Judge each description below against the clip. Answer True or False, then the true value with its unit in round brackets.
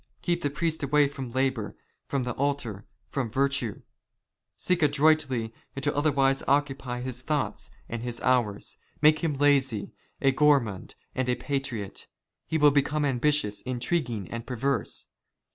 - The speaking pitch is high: False (135 Hz)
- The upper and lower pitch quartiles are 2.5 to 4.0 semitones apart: True (2.9 semitones)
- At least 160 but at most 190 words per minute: False (145 wpm)